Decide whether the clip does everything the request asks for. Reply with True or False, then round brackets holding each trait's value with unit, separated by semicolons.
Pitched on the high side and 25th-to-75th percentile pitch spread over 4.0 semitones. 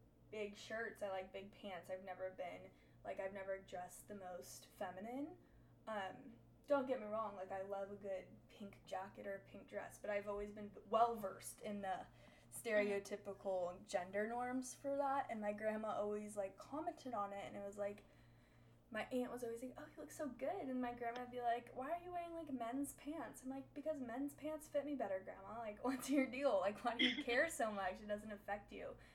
True (215 Hz; 4.6 semitones)